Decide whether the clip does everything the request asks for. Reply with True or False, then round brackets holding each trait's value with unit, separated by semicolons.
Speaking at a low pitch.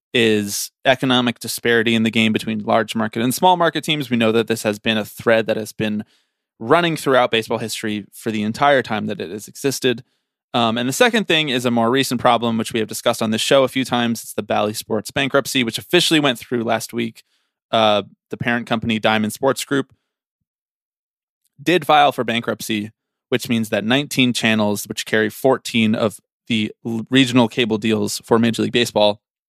True (115 Hz)